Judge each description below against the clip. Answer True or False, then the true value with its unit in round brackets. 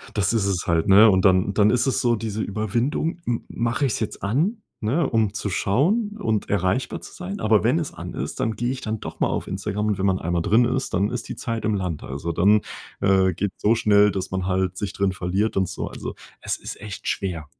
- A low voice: True (105 Hz)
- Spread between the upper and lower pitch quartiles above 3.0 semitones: True (3.7 semitones)